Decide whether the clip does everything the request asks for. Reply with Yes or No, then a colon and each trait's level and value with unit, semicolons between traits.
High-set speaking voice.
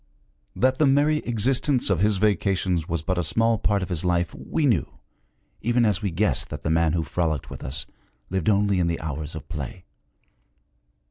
No: very low, 95 Hz